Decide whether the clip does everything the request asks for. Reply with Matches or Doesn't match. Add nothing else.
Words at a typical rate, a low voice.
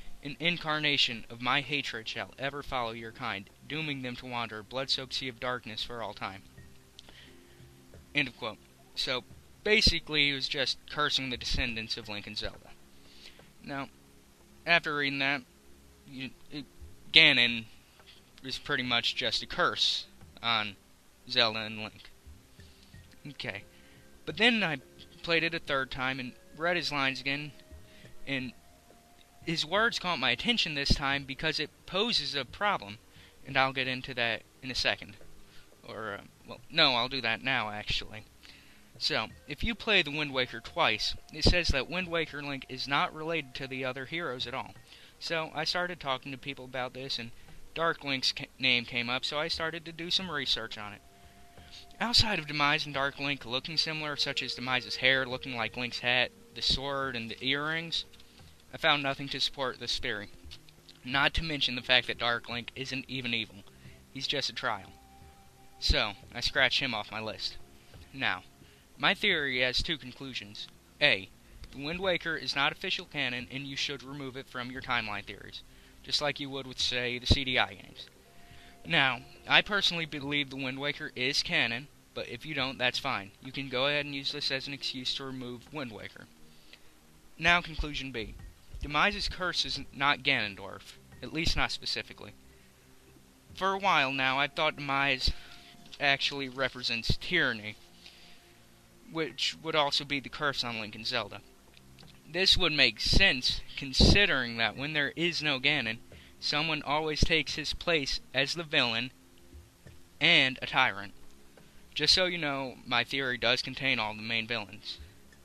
Matches